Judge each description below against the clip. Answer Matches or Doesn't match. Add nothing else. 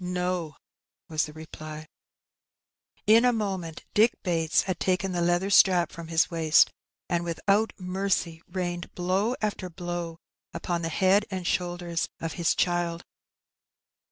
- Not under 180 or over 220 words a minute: Doesn't match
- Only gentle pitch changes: Matches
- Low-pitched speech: Doesn't match